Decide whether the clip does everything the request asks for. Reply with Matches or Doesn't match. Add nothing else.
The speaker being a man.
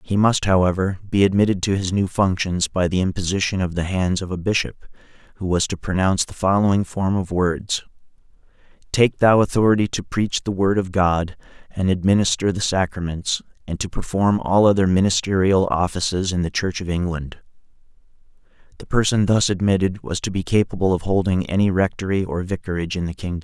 Matches